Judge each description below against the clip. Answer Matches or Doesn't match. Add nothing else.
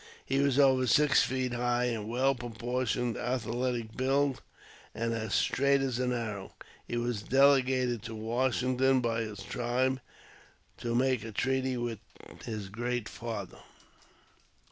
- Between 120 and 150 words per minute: Matches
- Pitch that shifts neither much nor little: Doesn't match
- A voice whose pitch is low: Matches